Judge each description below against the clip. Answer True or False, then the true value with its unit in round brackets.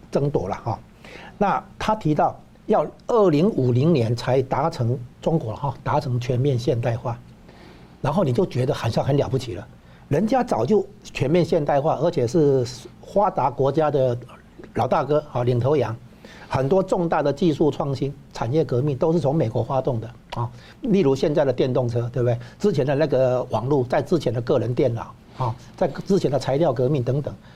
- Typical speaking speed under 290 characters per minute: True (270 characters per minute)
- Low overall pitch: True (130 Hz)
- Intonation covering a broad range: False (3.9 semitones)